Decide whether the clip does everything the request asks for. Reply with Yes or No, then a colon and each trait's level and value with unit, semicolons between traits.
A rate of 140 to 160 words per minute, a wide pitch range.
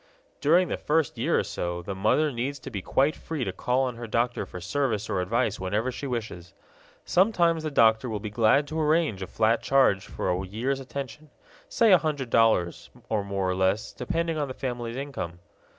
No: average, 200 wpm; wide, 5.9 semitones